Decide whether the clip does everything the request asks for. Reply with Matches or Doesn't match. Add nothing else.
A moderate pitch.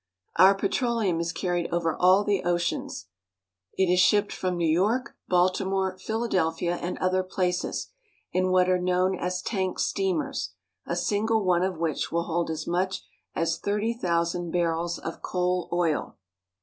Matches